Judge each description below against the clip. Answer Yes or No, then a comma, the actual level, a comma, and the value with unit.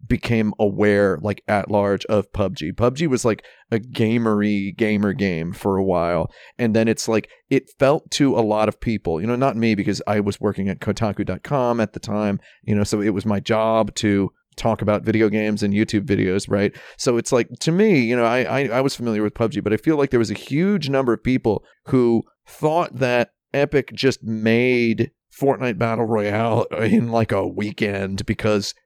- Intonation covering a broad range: No, average, 2.8 semitones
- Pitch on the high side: No, low, 110 Hz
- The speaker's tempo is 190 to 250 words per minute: Yes, average, 200 wpm